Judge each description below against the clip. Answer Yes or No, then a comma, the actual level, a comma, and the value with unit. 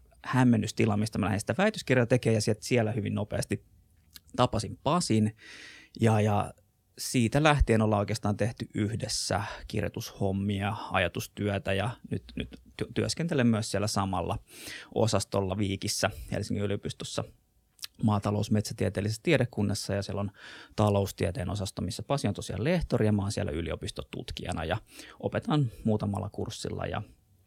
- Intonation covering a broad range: No, narrow, 2.4 semitones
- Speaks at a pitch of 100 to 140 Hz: Yes, low, 105 Hz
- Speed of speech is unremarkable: Yes, average, 125 wpm